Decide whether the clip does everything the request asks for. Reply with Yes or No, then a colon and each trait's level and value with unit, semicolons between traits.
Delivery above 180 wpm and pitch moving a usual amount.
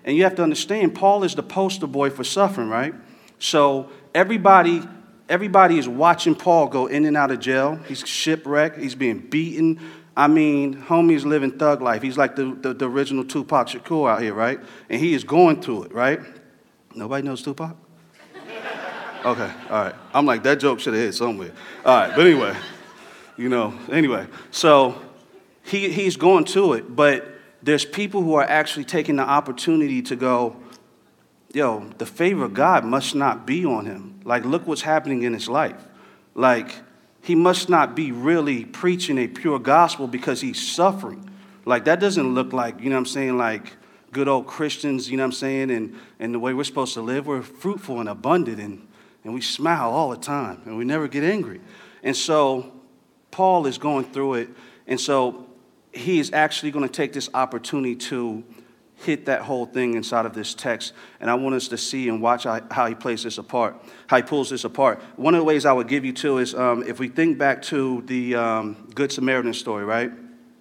Yes: average, 195 wpm; average, 4.5 semitones